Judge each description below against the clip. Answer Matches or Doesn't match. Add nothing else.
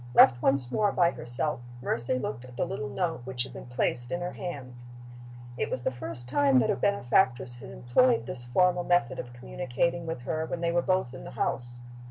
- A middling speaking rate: Doesn't match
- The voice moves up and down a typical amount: Doesn't match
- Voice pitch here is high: Doesn't match